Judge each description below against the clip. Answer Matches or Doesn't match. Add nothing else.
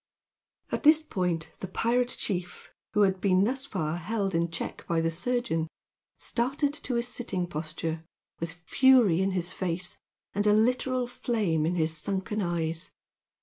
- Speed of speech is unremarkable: Matches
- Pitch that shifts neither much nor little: Doesn't match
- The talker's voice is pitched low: Doesn't match